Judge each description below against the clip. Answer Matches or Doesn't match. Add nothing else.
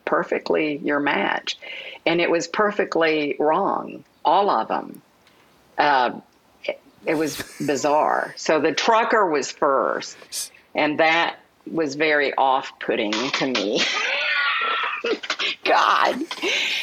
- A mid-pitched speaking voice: Matches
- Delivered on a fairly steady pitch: Matches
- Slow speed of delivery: Matches